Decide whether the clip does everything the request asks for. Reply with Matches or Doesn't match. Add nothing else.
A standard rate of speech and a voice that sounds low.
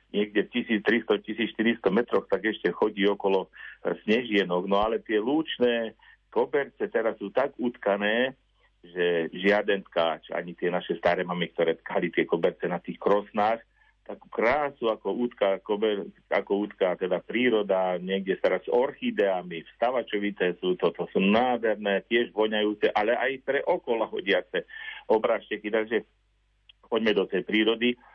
Matches